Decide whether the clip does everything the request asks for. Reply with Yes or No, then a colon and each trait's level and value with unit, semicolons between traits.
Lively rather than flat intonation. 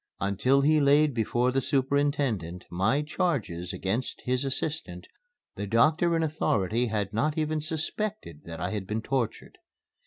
Yes: wide, 6.7 semitones